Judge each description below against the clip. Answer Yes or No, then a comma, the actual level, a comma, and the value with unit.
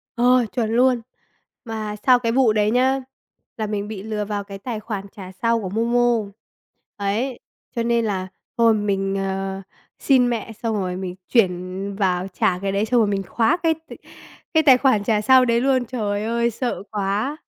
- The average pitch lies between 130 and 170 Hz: No, high, 220 Hz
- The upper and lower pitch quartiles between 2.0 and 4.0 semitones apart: Yes, average, 3.4 semitones